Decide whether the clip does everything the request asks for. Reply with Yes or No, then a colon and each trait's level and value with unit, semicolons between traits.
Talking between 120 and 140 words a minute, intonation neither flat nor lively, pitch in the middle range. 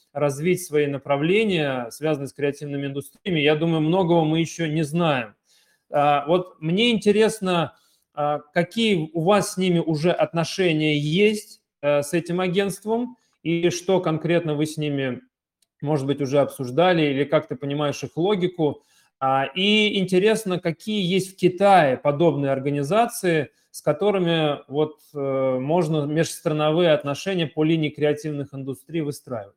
Yes: average, 130 wpm; average, 3.8 semitones; medium, 160 Hz